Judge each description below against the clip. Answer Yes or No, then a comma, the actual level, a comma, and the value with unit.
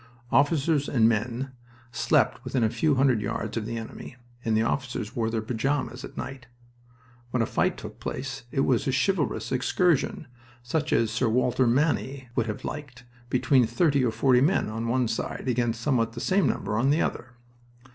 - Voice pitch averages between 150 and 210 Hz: No, low, 125 Hz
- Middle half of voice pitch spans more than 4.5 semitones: No, average, 3.2 semitones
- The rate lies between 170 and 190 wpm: Yes, average, 180 wpm